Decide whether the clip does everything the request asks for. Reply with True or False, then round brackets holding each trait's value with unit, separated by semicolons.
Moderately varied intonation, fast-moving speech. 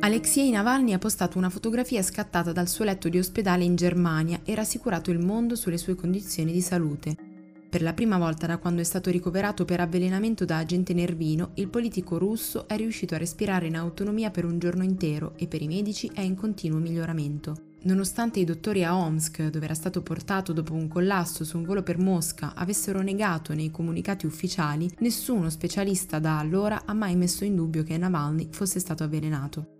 True (3.3 semitones; 190 wpm)